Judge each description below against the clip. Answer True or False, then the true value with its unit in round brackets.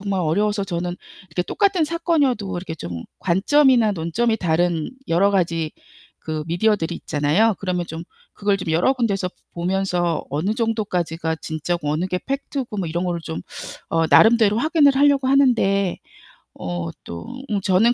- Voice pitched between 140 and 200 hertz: True (190 Hz)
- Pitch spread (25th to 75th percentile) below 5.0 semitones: False (5.4 semitones)